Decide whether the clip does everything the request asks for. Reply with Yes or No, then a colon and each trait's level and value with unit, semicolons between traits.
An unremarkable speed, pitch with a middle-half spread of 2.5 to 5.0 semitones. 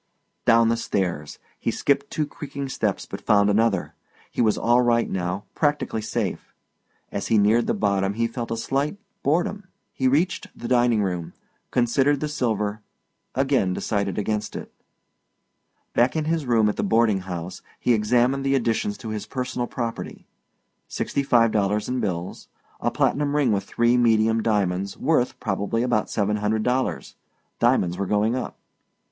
Yes: average, 160 wpm; average, 3.7 semitones